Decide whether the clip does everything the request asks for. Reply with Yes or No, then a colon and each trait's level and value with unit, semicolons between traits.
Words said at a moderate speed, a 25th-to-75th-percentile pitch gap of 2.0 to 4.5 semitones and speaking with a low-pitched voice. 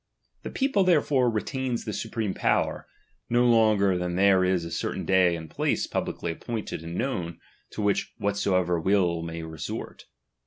No: average, 155 wpm; average, 4.9 semitones; low, 100 Hz